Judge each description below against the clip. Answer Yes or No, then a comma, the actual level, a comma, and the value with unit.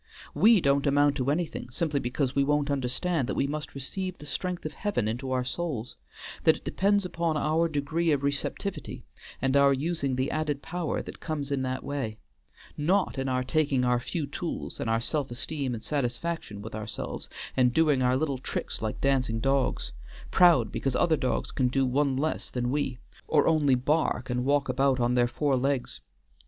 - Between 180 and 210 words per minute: Yes, average, 190 wpm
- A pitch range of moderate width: Yes, average, 3.4 semitones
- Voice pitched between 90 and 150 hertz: Yes, medium, 140 Hz